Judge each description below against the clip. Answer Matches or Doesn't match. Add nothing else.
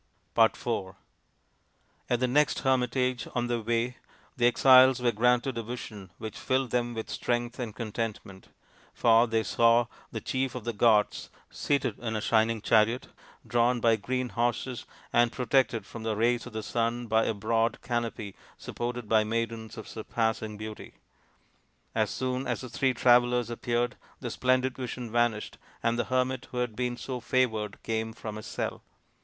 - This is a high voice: Doesn't match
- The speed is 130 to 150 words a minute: Doesn't match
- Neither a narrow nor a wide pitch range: Doesn't match